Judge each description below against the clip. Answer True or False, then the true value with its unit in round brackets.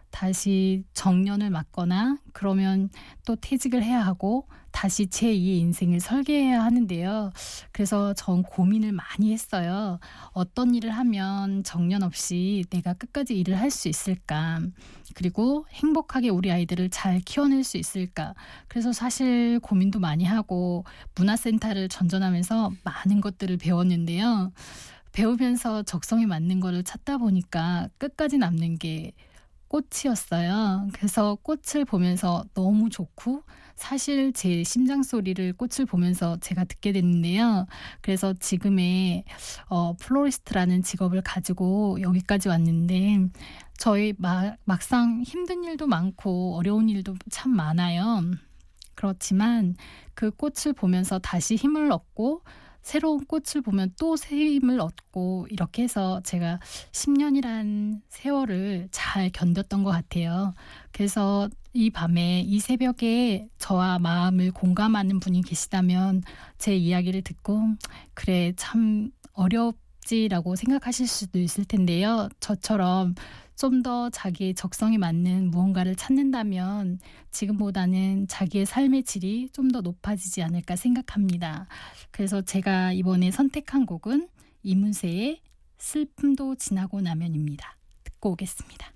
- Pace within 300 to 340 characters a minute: False (275 characters per minute)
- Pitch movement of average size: True (4.3 semitones)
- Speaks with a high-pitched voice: True (195 Hz)